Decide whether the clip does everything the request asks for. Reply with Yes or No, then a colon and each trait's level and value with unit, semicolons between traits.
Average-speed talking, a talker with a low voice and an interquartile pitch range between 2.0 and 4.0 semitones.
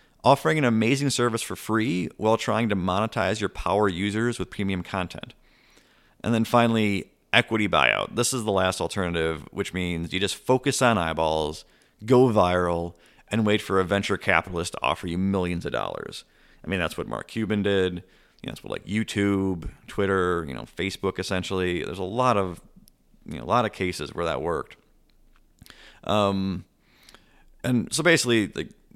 Yes: average, 170 wpm; low, 100 Hz; average, 3.7 semitones